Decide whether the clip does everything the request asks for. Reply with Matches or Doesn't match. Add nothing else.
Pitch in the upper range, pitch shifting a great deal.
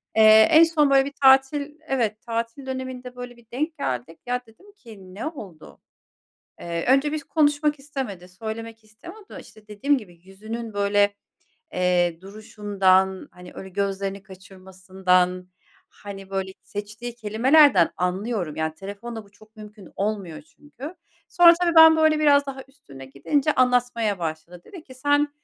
Matches